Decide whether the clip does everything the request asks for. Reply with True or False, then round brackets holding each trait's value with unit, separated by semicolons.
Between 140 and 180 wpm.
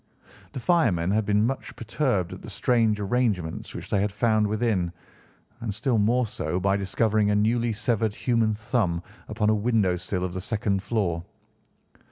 True (170 wpm)